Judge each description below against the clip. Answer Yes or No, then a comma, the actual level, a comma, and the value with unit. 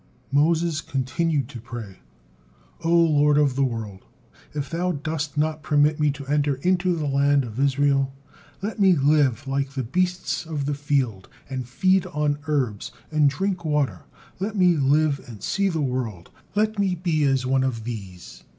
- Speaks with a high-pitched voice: No, medium, 145 Hz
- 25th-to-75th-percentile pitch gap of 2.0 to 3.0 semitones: No, average, 3.7 semitones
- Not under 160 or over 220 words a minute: Yes, average, 170 wpm